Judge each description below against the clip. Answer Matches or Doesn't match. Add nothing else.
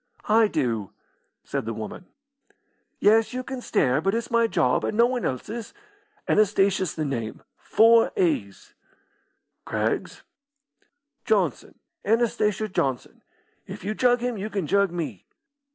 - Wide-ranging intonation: Matches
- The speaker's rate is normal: Doesn't match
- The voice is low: Doesn't match